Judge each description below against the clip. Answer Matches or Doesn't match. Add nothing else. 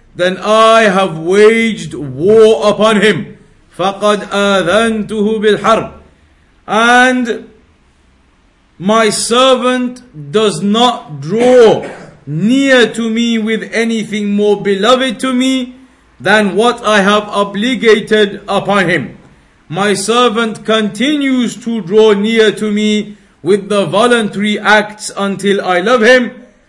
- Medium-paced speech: Doesn't match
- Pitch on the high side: Matches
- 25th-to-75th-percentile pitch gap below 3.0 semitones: Matches